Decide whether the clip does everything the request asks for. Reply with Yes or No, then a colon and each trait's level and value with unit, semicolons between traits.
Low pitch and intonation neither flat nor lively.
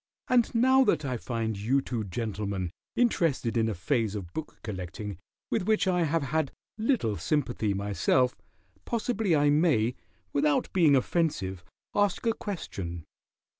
No: low, 130 Hz; wide, 8.8 semitones